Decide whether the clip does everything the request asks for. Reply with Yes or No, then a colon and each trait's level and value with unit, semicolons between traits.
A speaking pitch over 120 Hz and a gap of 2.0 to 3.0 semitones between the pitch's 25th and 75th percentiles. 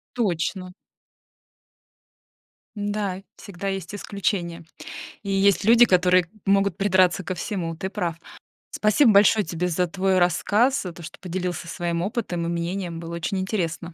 Yes: medium, 185 Hz; narrow, 2.6 semitones